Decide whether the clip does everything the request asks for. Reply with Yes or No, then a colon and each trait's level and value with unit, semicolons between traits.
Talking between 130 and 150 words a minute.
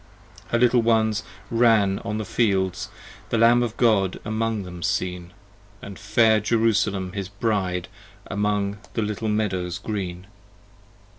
Yes: slow, 135 wpm